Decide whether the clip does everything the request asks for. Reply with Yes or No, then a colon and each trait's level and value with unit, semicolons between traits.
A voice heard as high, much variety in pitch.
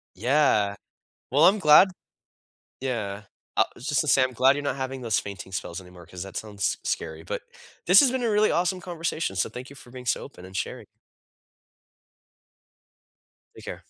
No: low, 130 Hz; wide, 7.4 semitones